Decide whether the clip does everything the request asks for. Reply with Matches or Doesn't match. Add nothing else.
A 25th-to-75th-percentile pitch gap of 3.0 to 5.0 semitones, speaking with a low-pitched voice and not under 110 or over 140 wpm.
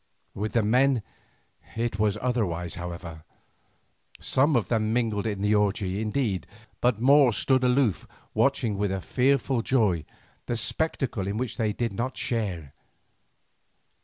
Matches